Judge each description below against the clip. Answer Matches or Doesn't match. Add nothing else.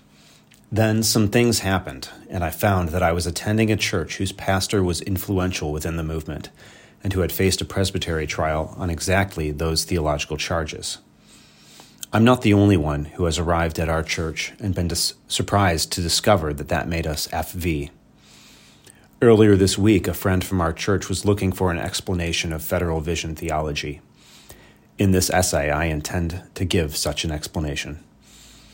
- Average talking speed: Matches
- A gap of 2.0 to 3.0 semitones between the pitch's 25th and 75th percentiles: Doesn't match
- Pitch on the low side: Matches